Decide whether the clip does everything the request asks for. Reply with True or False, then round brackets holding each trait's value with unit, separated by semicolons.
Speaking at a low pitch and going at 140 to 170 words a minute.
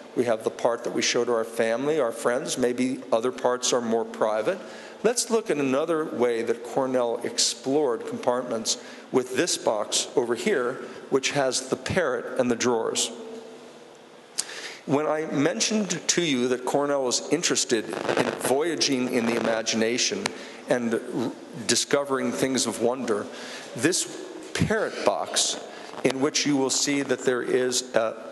True (130 Hz; 155 wpm)